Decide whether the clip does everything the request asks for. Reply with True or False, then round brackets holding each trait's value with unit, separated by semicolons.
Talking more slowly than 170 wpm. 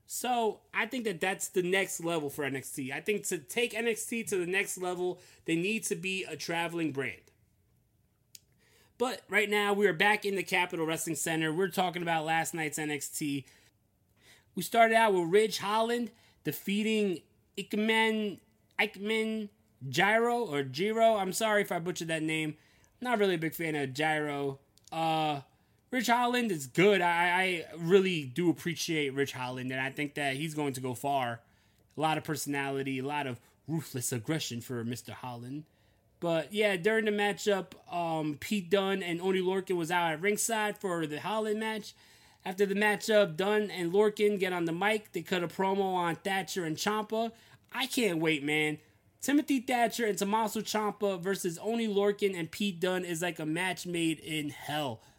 False (175 wpm)